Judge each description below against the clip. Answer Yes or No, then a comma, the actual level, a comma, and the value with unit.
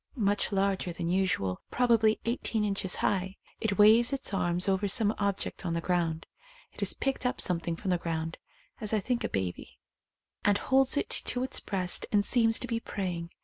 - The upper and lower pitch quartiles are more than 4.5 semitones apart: No, average, 4.2 semitones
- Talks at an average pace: Yes, average, 190 wpm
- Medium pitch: No, high, 200 Hz